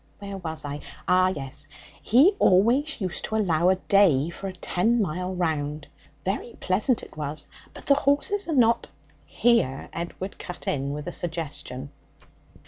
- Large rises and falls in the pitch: Yes, wide, 6.2 semitones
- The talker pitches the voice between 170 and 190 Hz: Yes, medium, 185 Hz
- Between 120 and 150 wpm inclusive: No, average, 160 wpm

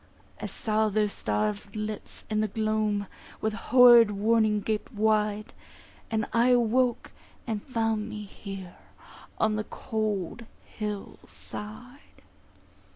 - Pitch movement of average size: No, narrow, 1.2 semitones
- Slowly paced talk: Yes, slow, 115 wpm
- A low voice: No, high, 215 Hz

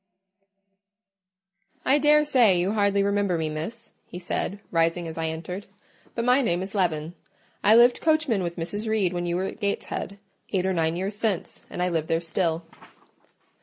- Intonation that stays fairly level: No, average, 4.3 semitones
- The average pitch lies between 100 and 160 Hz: No, high, 190 Hz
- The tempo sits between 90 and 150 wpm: No, average, 170 wpm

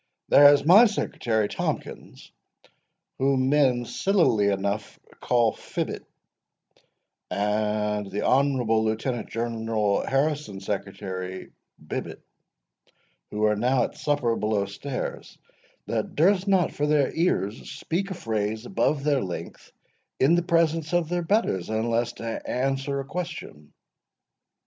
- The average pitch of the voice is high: No, low, 125 Hz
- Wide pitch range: Yes, wide, 5.9 semitones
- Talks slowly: Yes, slow, 120 wpm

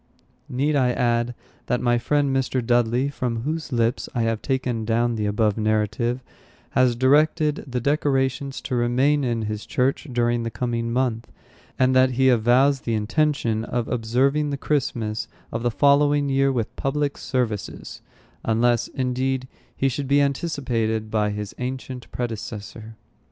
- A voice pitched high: No, low, 125 Hz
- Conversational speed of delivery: Yes, average, 150 wpm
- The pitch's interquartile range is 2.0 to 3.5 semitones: Yes, average, 2.9 semitones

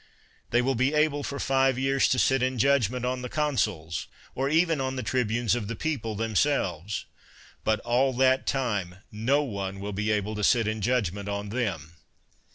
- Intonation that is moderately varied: Yes, average, 4.3 semitones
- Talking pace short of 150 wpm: No, average, 180 wpm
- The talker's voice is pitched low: Yes, low, 120 Hz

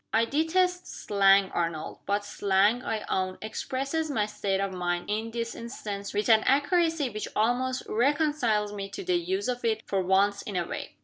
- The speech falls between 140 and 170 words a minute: No, average, 180 wpm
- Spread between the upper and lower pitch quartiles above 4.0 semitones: Yes, wide, 5.5 semitones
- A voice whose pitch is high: Yes, high, 220 Hz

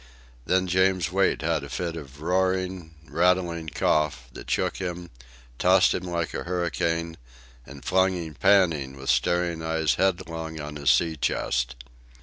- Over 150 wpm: No, average, 145 wpm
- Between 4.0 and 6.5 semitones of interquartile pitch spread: No, average, 2.9 semitones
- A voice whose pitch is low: Yes, very low, 85 Hz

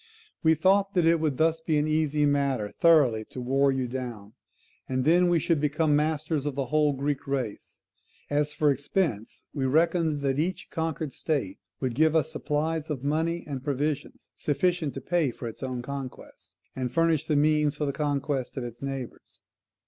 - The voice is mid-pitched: Yes, medium, 145 Hz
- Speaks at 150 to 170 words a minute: No, average, 185 wpm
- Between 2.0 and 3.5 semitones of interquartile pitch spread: Yes, average, 3.0 semitones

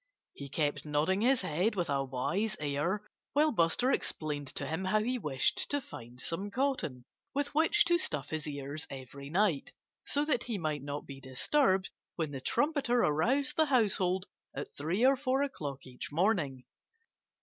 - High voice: No, medium, 175 Hz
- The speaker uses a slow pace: No, average, 170 wpm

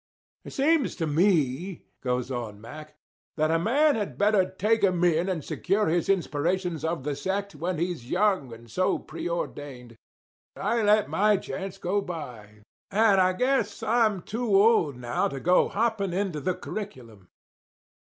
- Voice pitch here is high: No, medium, 180 Hz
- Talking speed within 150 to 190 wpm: Yes, average, 155 wpm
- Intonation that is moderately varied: No, wide, 5.8 semitones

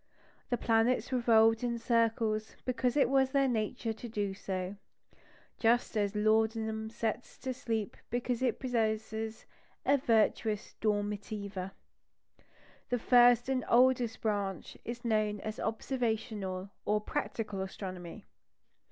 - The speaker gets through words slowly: Yes, slow, 115 wpm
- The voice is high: Yes, high, 225 Hz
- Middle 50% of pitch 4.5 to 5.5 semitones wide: No, narrow, 2.4 semitones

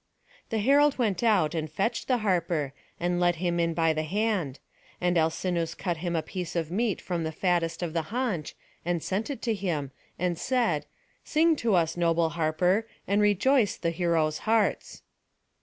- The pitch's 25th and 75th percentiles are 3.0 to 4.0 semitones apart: No, average, 4.4 semitones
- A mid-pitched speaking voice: Yes, medium, 175 Hz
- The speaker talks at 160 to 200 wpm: Yes, average, 175 wpm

